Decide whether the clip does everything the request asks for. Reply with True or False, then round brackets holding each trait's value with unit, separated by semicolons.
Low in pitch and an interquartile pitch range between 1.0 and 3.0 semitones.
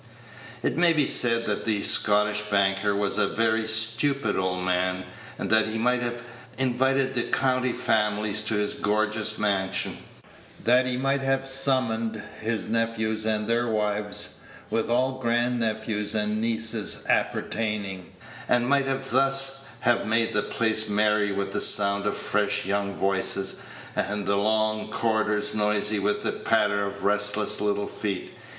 True (110 Hz; 2.4 semitones)